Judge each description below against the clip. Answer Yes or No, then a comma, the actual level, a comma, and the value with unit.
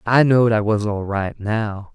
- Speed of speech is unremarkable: No, fast, 215 wpm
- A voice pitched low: Yes, low, 110 Hz